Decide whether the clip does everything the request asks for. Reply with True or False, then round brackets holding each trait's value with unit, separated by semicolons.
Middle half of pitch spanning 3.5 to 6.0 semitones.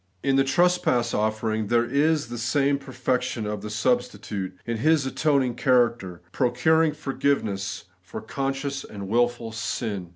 True (4.1 semitones)